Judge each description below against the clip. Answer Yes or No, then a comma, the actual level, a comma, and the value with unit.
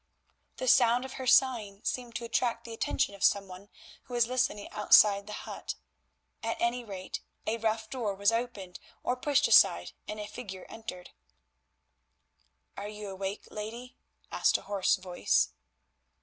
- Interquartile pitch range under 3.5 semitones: Yes, average, 3.1 semitones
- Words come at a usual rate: Yes, average, 155 wpm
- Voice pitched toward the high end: Yes, high, 220 Hz